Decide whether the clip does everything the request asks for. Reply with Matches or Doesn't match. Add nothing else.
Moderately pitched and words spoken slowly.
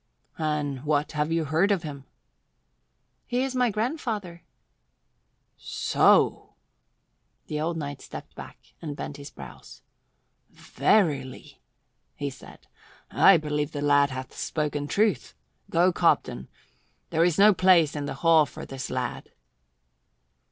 Matches